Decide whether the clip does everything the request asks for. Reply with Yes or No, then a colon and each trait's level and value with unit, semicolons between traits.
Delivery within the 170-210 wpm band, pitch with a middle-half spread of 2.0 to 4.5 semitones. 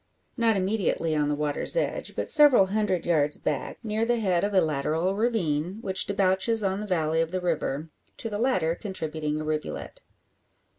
No: average, 180 wpm; average, 5.2 semitones